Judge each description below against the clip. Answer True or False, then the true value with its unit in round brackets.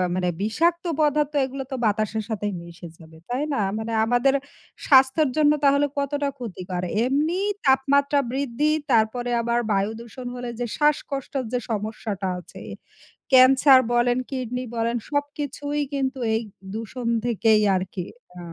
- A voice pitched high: True (250 Hz)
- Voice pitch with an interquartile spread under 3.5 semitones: False (4.3 semitones)